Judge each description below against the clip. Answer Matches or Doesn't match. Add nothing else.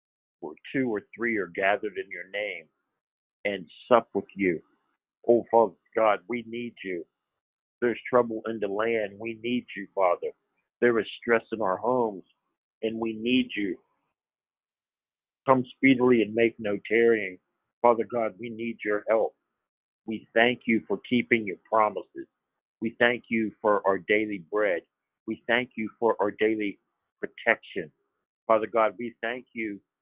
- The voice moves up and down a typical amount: Doesn't match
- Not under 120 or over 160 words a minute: Matches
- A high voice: Doesn't match